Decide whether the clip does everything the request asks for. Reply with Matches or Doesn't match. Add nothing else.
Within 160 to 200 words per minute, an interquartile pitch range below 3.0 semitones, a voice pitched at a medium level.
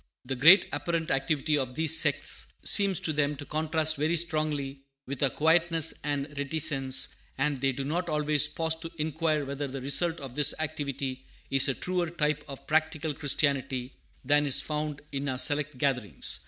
Matches